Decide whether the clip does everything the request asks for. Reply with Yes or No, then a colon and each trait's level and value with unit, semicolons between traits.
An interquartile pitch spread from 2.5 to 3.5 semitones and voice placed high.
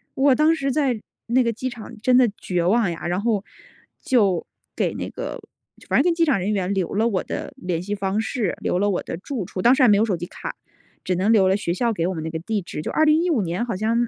No: average, 5.1 semitones; high, 210 Hz